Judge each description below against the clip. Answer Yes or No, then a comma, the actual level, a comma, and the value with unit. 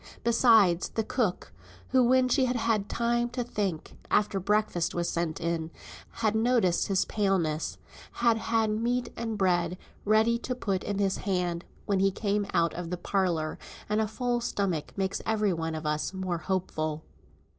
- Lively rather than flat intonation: No, average, 4.6 semitones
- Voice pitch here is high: Yes, high, 200 Hz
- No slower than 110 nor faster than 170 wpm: Yes, average, 165 wpm